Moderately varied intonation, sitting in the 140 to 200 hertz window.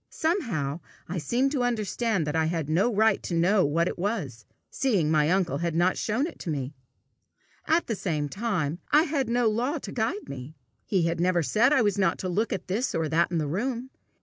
No: wide, 6.5 semitones; medium, 185 Hz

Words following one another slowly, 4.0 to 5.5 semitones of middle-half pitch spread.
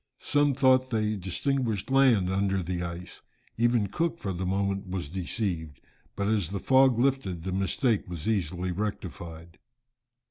No: average, 145 wpm; average, 4.9 semitones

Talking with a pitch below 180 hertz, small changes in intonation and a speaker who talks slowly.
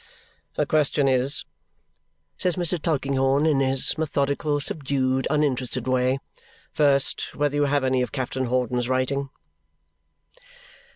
Yes: low, 135 Hz; narrow, 2.1 semitones; slow, 115 wpm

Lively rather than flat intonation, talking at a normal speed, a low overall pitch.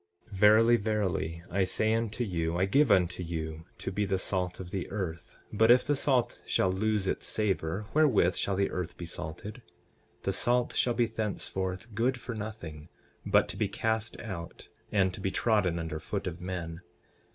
No: average, 3.9 semitones; average, 185 wpm; very low, 95 Hz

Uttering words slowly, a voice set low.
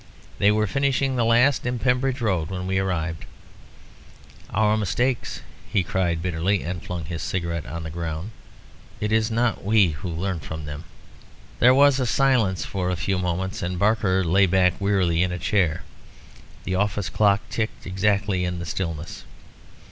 No: average, 165 wpm; very low, 95 Hz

